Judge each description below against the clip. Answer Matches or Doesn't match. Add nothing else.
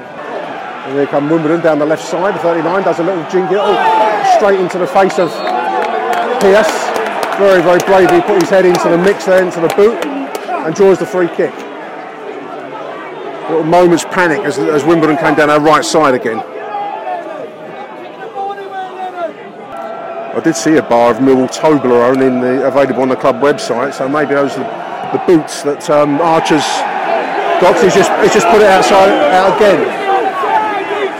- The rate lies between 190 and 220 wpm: Doesn't match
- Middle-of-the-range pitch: Matches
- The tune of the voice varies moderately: Doesn't match